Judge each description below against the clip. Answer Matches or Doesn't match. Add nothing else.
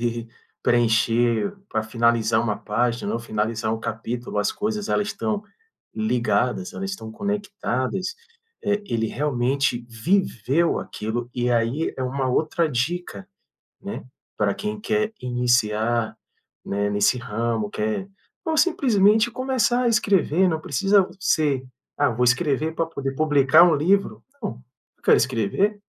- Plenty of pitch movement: Matches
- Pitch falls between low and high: Doesn't match